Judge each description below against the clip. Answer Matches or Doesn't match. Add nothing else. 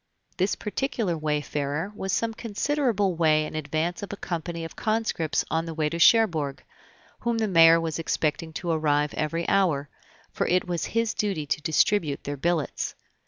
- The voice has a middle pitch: Matches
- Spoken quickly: Doesn't match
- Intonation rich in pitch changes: Doesn't match